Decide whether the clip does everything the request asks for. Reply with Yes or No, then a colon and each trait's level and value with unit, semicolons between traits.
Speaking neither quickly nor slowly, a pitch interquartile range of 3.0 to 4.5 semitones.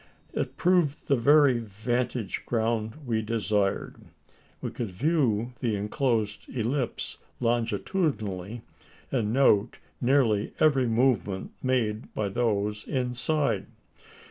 No: slow, 100 wpm; average, 3.7 semitones